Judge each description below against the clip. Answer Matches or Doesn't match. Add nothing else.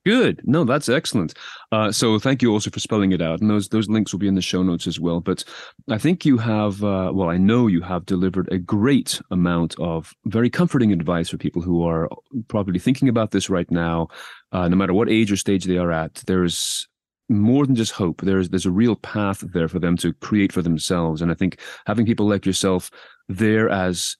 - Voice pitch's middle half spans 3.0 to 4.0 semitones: Matches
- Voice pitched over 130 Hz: Doesn't match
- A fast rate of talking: Matches